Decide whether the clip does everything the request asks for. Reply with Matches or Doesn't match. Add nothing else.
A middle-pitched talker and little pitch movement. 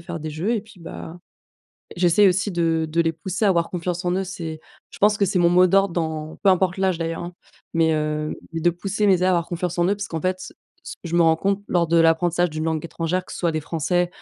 Matches